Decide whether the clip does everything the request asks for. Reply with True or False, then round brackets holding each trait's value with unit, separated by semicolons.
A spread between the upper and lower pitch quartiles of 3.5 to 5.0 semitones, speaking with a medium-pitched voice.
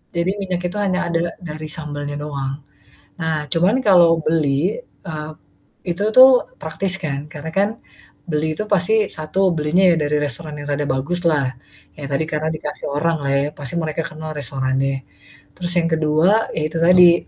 False (3.0 semitones; 155 Hz)